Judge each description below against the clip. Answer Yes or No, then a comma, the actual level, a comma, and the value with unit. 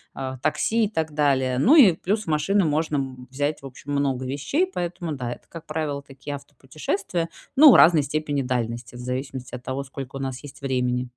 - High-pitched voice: No, medium, 140 Hz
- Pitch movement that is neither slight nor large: Yes, average, 3.6 semitones